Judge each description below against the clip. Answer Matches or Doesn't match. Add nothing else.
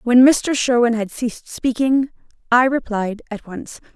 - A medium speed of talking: Matches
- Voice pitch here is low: Doesn't match